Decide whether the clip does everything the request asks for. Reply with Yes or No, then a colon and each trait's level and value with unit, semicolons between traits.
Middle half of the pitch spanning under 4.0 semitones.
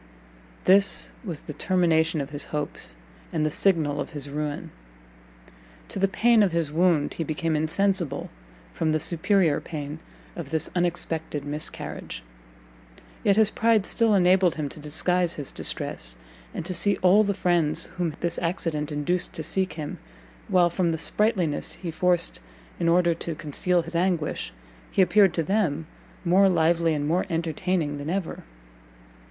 Yes: average, 3.2 semitones